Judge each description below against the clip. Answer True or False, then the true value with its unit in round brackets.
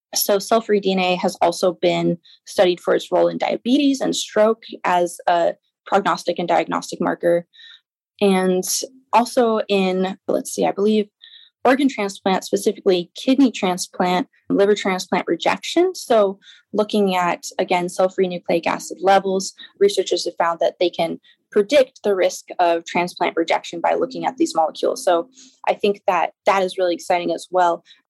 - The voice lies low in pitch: False (195 Hz)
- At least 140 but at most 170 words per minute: True (155 wpm)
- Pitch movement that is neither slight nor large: True (3.6 semitones)